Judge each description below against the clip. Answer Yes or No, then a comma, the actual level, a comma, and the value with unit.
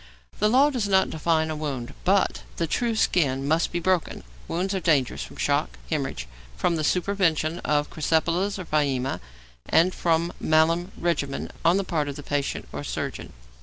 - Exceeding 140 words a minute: Yes, average, 170 wpm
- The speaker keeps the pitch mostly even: No, average, 3.7 semitones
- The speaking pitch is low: No, medium, 165 Hz